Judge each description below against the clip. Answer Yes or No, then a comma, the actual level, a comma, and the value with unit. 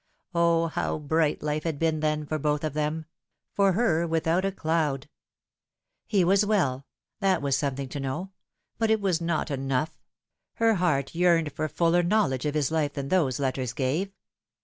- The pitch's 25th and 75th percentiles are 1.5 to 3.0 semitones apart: No, average, 3.6 semitones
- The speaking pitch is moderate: Yes, medium, 155 Hz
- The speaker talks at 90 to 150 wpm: No, average, 170 wpm